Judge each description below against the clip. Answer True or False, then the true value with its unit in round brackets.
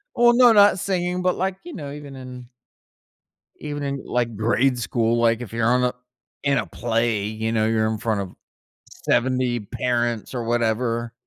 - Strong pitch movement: False (3.8 semitones)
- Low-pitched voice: True (120 Hz)